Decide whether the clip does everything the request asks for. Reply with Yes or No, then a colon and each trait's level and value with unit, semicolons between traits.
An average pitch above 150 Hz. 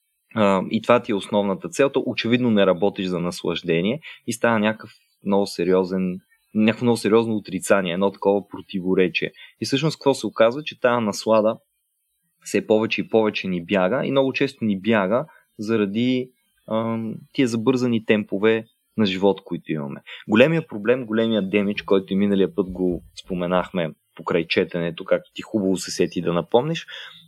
No: low, 110 Hz